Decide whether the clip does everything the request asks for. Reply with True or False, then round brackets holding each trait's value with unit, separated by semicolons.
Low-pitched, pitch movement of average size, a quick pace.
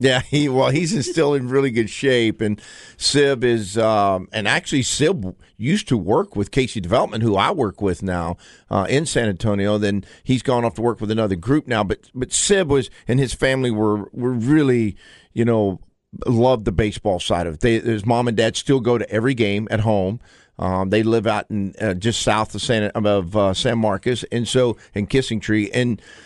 True (115 Hz; 3.5 semitones; 210 wpm)